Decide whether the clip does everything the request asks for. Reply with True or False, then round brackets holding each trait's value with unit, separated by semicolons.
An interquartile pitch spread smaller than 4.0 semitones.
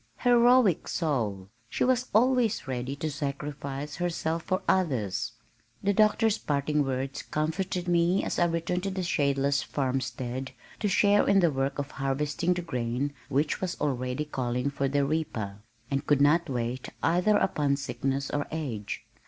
False (4.7 semitones)